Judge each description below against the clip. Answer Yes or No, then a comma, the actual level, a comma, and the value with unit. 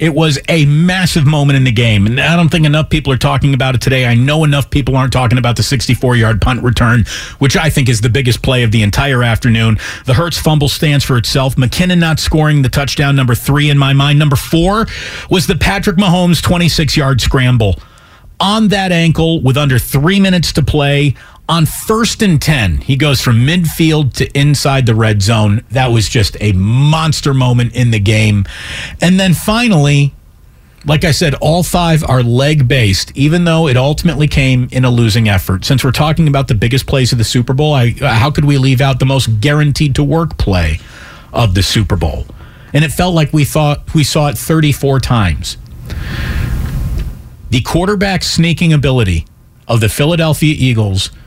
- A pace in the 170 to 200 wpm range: Yes, average, 190 wpm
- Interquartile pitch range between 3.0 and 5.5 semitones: Yes, average, 4.4 semitones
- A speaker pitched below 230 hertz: Yes, medium, 140 Hz